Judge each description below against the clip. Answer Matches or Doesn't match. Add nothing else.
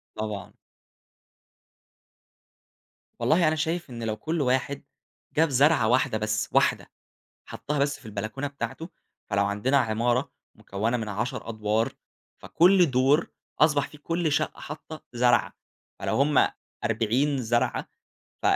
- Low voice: Matches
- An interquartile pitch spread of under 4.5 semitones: Doesn't match